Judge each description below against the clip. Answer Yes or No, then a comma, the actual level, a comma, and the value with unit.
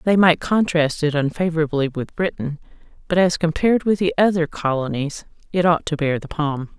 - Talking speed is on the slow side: No, average, 175 wpm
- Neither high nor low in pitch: Yes, medium, 160 Hz